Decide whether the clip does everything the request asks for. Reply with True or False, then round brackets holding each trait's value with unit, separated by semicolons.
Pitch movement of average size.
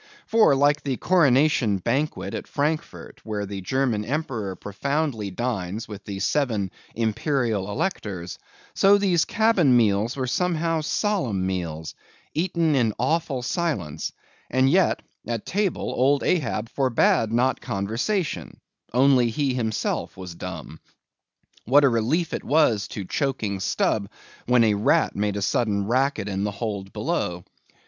False (6.4 semitones)